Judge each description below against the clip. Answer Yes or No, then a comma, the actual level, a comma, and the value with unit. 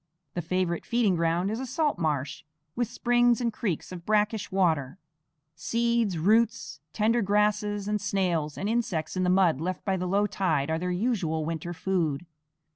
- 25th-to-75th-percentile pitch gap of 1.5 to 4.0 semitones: No, average, 4.7 semitones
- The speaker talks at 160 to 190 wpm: Yes, average, 170 wpm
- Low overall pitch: No, high, 190 Hz